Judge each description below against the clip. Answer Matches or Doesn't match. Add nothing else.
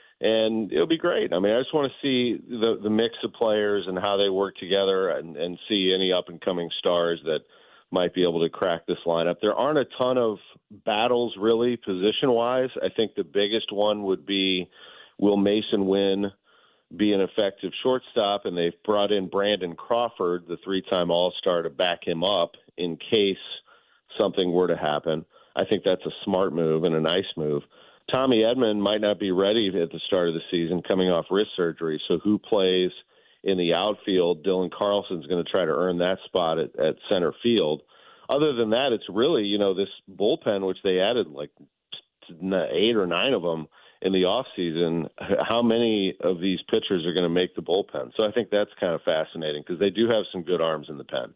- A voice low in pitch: Matches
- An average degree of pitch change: Matches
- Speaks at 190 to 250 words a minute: Matches